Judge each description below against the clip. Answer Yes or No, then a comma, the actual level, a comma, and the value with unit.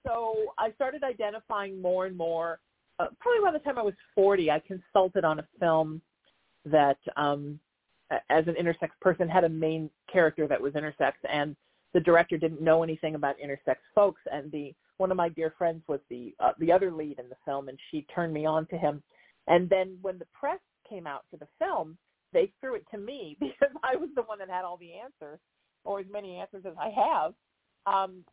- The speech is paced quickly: Yes, fast, 210 wpm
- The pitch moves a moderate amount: Yes, average, 4.1 semitones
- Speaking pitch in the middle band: Yes, medium, 175 Hz